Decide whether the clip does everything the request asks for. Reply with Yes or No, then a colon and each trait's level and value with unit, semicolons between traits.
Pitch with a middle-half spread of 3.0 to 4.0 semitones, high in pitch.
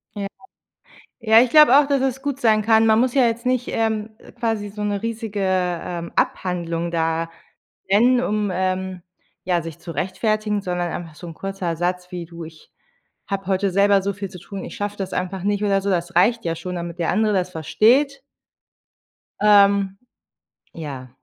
Yes: average, 3.7 semitones; high, 195 Hz